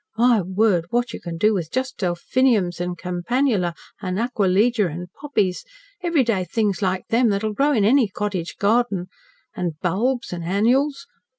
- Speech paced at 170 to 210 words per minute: No, average, 155 wpm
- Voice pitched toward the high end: Yes, high, 205 Hz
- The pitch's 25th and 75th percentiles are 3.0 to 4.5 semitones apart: No, average, 5.1 semitones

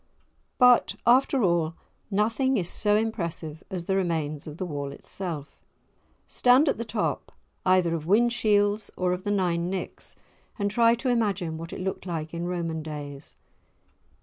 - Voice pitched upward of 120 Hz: Yes, medium, 185 Hz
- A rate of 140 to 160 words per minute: Yes, average, 155 wpm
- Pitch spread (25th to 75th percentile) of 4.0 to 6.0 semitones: Yes, average, 4.8 semitones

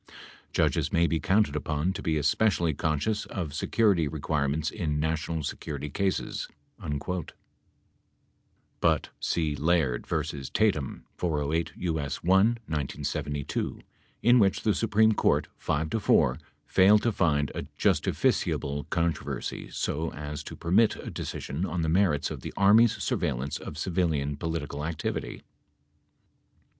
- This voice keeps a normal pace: No, slow, 130 wpm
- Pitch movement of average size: Yes, average, 4.5 semitones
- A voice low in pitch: Yes, very low, 80 Hz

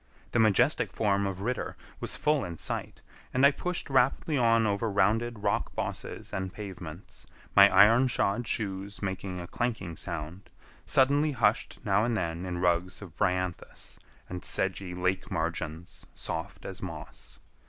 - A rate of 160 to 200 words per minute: No, average, 150 wpm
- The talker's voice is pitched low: Yes, low, 100 Hz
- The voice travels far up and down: No, average, 4.3 semitones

